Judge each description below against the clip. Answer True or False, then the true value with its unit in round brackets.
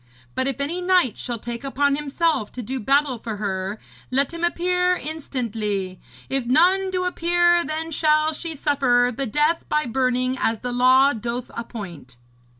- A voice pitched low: False (270 Hz)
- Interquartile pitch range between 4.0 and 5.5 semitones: True (5.2 semitones)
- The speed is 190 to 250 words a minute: False (160 wpm)